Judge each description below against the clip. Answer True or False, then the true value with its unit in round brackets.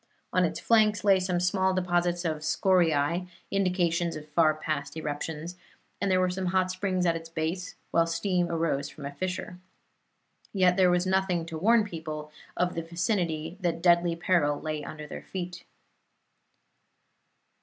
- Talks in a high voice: False (175 Hz)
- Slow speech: False (160 wpm)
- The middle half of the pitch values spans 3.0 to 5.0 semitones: False (2.4 semitones)